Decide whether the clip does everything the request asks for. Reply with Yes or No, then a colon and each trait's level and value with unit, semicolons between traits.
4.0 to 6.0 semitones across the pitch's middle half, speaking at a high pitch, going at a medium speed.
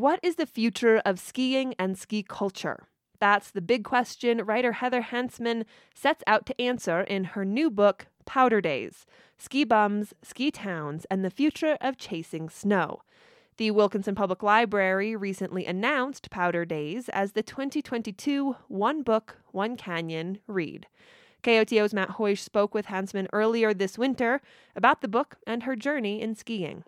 Yes: average, 4.3 semitones; high, 215 Hz; average, 155 wpm